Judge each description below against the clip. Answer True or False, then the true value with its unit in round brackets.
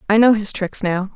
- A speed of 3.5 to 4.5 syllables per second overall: False (5.2 syllables/s)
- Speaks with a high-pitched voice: True (205 Hz)